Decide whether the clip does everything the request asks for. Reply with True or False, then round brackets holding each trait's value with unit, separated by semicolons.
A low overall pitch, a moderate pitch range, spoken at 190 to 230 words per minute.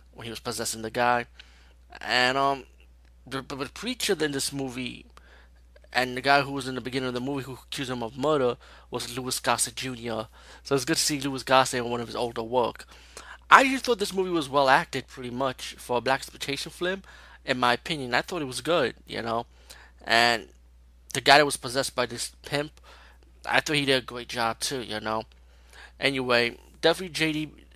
True (130 Hz; 3.4 semitones; 205 wpm)